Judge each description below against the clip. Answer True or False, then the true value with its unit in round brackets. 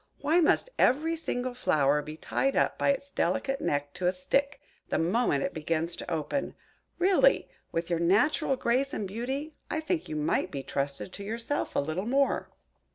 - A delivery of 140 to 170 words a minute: False (180 wpm)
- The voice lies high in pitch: True (230 Hz)